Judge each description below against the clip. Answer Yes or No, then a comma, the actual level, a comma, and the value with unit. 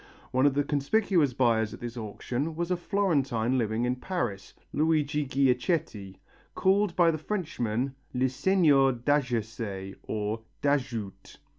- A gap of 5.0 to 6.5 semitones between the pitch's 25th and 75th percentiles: Yes, average, 5.3 semitones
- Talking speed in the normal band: No, slow, 130 wpm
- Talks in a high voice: No, low, 135 Hz